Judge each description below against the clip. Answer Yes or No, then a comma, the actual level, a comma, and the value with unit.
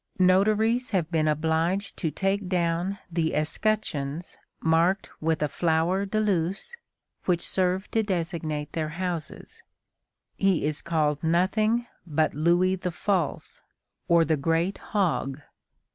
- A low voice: No, medium, 170 Hz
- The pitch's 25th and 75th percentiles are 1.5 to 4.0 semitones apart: Yes, average, 3.3 semitones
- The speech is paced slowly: Yes, slow, 125 wpm